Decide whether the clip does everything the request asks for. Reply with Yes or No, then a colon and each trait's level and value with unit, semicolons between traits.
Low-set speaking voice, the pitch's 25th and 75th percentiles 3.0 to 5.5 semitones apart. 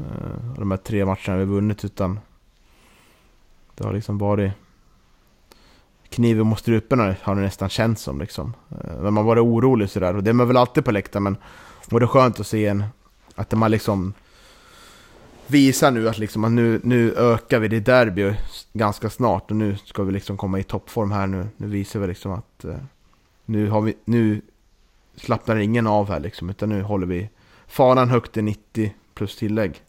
No: low, 105 Hz; narrow, 2.6 semitones